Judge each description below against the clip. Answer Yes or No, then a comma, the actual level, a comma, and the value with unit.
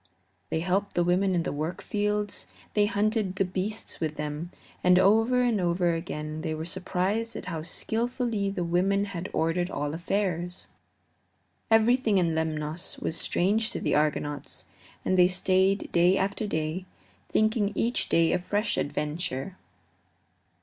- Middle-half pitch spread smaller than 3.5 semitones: No, average, 3.8 semitones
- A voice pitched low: No, medium, 185 Hz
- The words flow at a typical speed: Yes, average, 155 wpm